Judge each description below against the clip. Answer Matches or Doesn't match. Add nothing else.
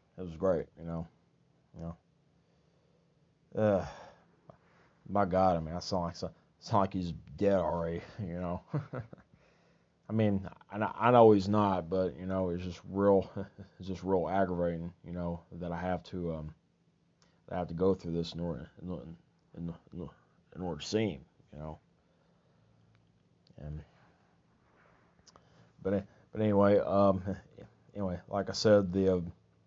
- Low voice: Matches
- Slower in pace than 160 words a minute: Matches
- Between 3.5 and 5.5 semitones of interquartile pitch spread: Doesn't match